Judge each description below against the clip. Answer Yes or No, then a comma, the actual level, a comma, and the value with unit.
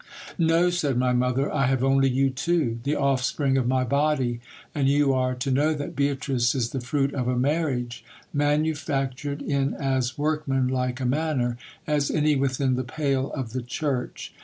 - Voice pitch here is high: No, low, 135 Hz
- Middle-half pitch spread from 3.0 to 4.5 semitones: No, narrow, 2.4 semitones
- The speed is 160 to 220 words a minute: Yes, average, 170 wpm